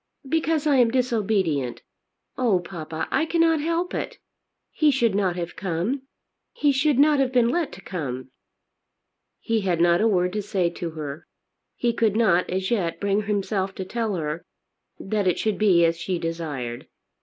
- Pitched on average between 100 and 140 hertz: No, high, 195 Hz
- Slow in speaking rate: No, average, 170 wpm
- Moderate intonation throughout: No, wide, 6.3 semitones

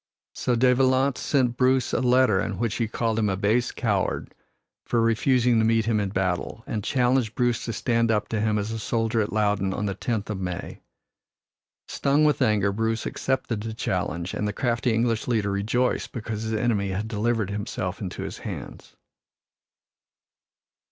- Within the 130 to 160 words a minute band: No, average, 180 wpm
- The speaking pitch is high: No, low, 110 Hz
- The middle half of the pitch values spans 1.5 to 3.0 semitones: Yes, average, 2.7 semitones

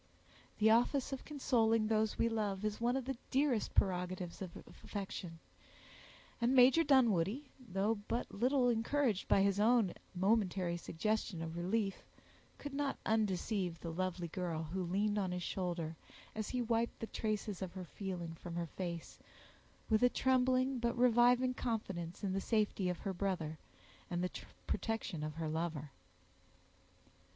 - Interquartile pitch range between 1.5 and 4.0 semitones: No, average, 4.9 semitones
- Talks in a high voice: Yes, high, 205 Hz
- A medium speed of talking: Yes, average, 150 wpm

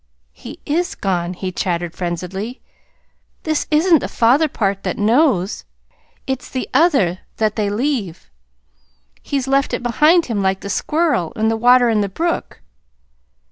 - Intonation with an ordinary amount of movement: No, wide, 6.9 semitones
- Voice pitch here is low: No, high, 225 Hz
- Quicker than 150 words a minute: No, average, 145 wpm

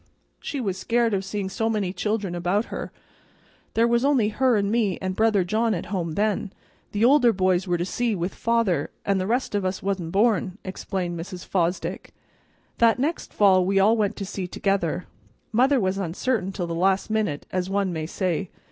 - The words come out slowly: No, average, 190 wpm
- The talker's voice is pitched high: Yes, high, 195 Hz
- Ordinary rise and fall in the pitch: Yes, average, 3.4 semitones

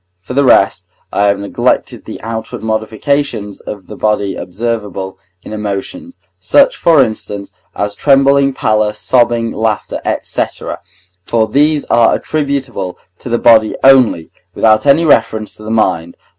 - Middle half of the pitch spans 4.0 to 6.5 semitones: Yes, average, 4.7 semitones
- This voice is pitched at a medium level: No, low, 110 Hz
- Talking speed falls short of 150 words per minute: Yes, average, 140 wpm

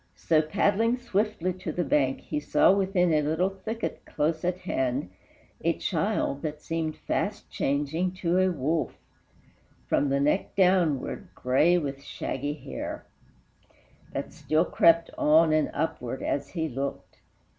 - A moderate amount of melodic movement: Yes, average, 4.1 semitones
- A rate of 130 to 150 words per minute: Yes, average, 140 wpm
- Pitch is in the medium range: Yes, medium, 160 Hz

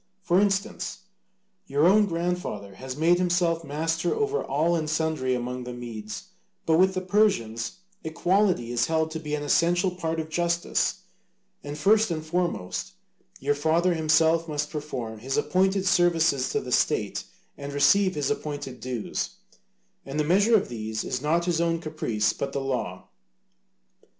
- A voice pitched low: No, medium, 160 Hz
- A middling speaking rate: Yes, average, 155 wpm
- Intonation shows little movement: No, average, 4.3 semitones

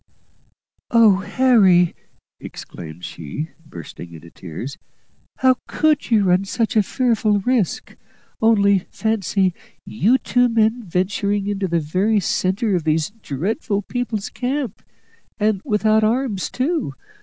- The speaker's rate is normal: No, slow, 120 wpm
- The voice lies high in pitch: Yes, high, 205 Hz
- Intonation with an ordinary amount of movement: Yes, average, 4.2 semitones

